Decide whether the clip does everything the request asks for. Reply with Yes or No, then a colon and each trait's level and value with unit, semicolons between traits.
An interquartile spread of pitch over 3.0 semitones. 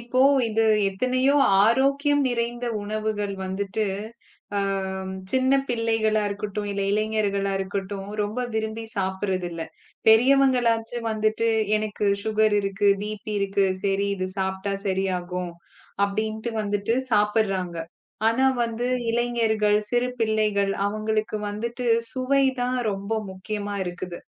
No: average, 2.7 semitones